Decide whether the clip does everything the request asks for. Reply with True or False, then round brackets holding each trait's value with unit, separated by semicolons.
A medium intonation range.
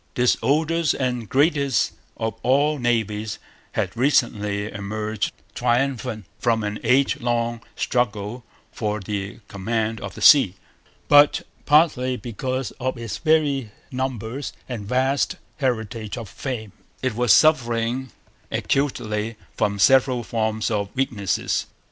True (3.6 semitones)